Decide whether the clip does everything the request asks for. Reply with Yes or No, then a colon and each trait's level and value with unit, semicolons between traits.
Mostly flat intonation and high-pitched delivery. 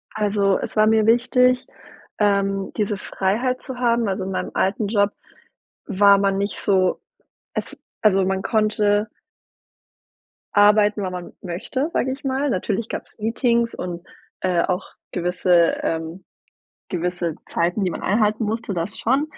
No: average, 3.1 semitones; high, 205 Hz